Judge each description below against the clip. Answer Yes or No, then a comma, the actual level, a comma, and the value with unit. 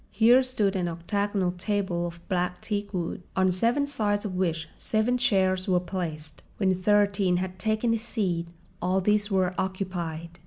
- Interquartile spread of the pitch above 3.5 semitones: No, average, 2.7 semitones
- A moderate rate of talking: Yes, average, 155 wpm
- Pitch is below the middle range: No, high, 190 Hz